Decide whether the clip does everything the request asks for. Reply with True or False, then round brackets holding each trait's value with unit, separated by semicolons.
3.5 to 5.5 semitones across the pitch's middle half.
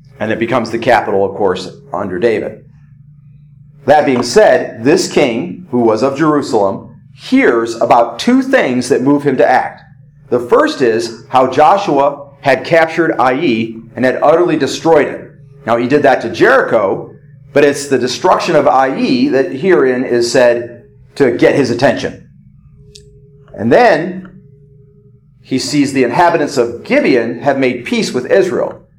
False (2.8 semitones)